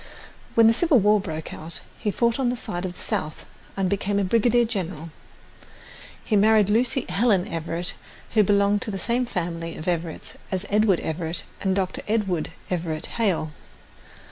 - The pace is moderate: Yes, average, 170 wpm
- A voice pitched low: No, high, 195 Hz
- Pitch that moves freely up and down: No, average, 4.3 semitones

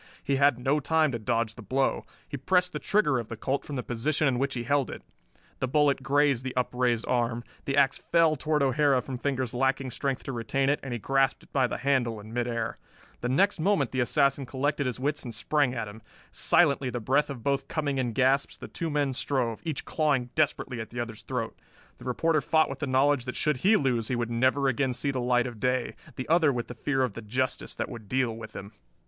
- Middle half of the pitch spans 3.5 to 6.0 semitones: No, average, 2.8 semitones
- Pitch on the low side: Yes, low, 130 Hz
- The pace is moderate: No, fast, 235 wpm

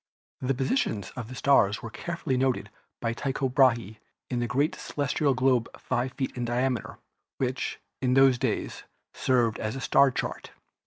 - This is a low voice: Yes, low, 130 Hz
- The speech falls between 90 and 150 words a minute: No, average, 160 wpm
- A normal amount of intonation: No, narrow, 2.1 semitones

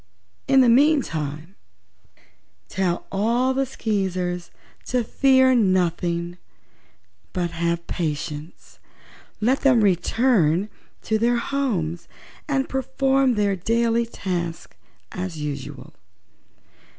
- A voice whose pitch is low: No, high, 200 Hz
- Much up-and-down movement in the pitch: Yes, wide, 6.6 semitones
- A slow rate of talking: Yes, slow, 90 wpm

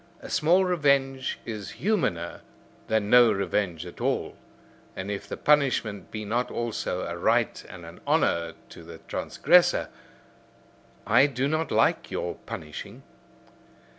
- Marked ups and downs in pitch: Yes, wide, 7.5 semitones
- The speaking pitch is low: Yes, low, 110 Hz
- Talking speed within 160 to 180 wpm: No, slow, 135 wpm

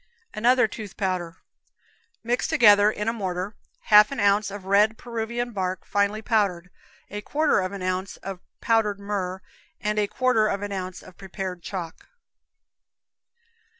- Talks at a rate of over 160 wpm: No, average, 150 wpm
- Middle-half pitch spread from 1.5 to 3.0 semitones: Yes, average, 2.7 semitones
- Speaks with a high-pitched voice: Yes, high, 205 Hz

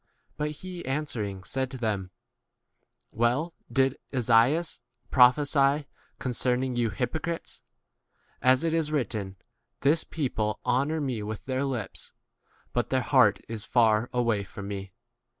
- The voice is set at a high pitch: No, low, 125 Hz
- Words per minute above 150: No, slow, 135 wpm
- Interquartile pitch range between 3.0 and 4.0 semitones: No, average, 4.6 semitones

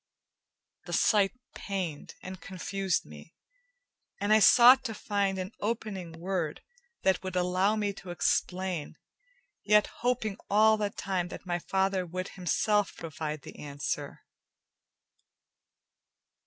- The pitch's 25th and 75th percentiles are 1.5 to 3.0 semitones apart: Yes, average, 2.7 semitones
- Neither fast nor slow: No, slow, 120 wpm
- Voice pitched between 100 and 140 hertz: No, high, 190 Hz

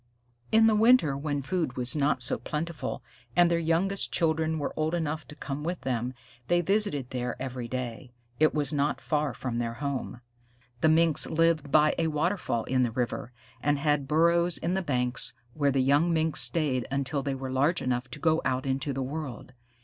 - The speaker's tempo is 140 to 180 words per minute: No, average, 190 wpm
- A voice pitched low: No, medium, 145 Hz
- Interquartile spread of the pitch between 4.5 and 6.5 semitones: No, average, 3.9 semitones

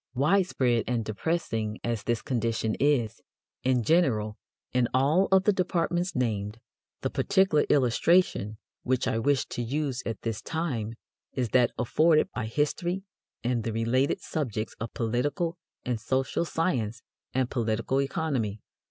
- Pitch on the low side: Yes, low, 125 Hz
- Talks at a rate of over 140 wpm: No, slow, 135 wpm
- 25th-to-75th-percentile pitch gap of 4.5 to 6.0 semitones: Yes, wide, 5.5 semitones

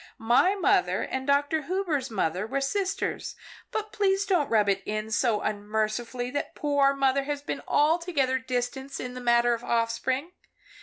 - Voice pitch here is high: Yes, very high, 265 Hz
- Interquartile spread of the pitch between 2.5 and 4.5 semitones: Yes, average, 4.1 semitones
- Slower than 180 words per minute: Yes, average, 155 wpm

